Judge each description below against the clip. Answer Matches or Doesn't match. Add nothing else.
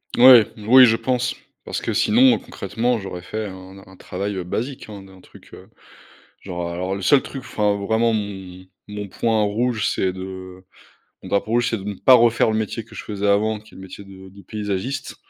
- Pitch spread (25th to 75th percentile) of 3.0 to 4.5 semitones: Matches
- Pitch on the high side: Doesn't match